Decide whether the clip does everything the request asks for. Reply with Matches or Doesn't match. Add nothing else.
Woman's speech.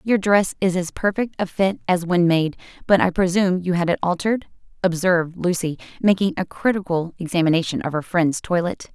Matches